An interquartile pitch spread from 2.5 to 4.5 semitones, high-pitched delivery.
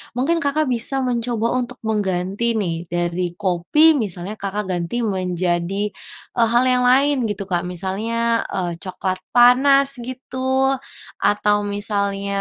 No: average, 5.1 semitones; high, 205 Hz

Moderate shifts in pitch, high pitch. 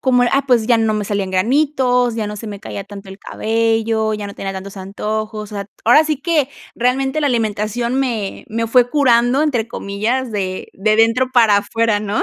Yes: average, 3.3 semitones; high, 225 Hz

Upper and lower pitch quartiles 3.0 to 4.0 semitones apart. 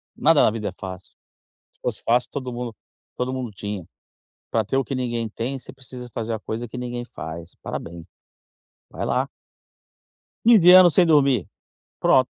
Yes: average, 3.6 semitones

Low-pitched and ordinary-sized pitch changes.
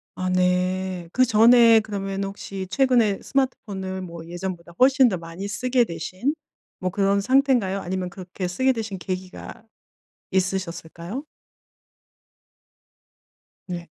No: high, 190 Hz; average, 3.9 semitones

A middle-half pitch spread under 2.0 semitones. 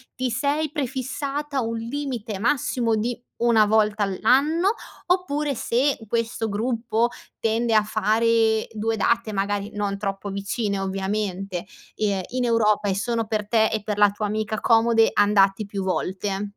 No: average, 2.7 semitones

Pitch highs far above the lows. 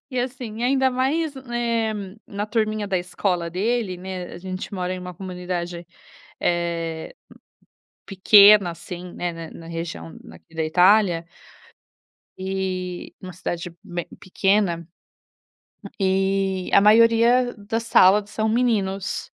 No: average, 3.7 semitones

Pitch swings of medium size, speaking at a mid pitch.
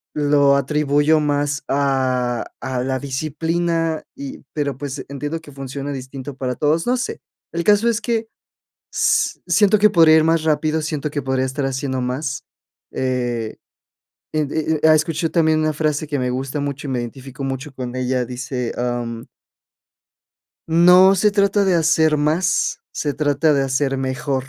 Yes: average, 3.2 semitones; medium, 145 Hz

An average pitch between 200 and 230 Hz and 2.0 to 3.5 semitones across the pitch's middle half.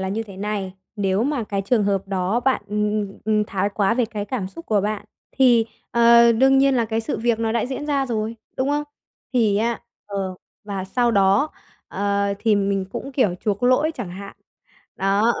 Yes: high, 215 Hz; average, 3.2 semitones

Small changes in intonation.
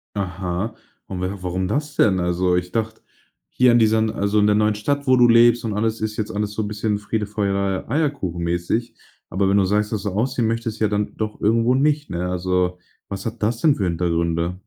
No: average, 3.5 semitones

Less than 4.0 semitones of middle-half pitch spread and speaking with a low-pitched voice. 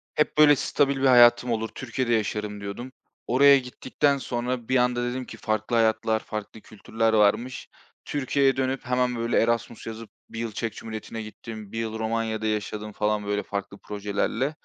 Yes: average, 2.7 semitones; low, 115 Hz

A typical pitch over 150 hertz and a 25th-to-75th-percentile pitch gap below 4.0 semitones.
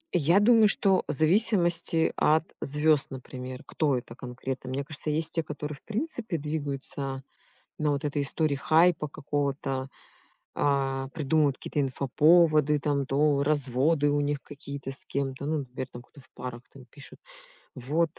No: medium, 145 Hz; narrow, 2.6 semitones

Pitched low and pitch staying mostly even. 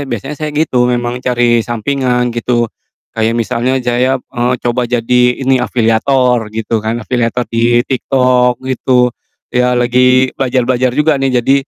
Yes: low, 125 Hz; narrow, 1.3 semitones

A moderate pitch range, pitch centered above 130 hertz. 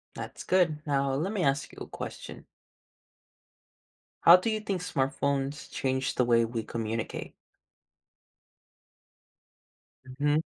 Yes: average, 4.5 semitones; medium, 140 Hz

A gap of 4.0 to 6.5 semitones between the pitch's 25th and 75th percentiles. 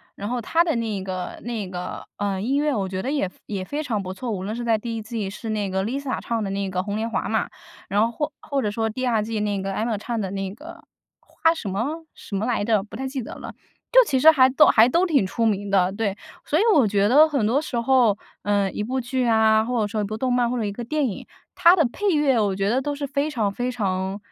Yes: average, 4.5 semitones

